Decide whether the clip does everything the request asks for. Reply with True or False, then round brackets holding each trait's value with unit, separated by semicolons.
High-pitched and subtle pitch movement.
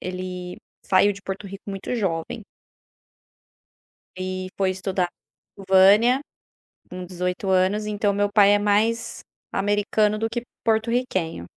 True (200 Hz; 2.2 semitones)